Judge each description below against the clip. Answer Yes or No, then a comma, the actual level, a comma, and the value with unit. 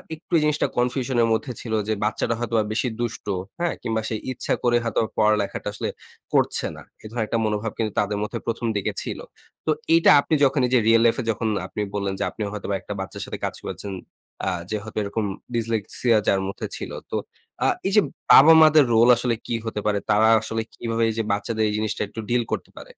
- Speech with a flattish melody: Yes, narrow, 2.3 semitones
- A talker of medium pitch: No, low, 115 Hz